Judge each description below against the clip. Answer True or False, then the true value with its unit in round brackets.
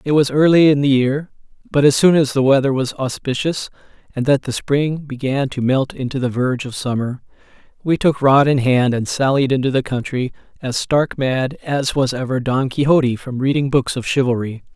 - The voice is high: False (135 Hz)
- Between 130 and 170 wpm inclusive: False (200 wpm)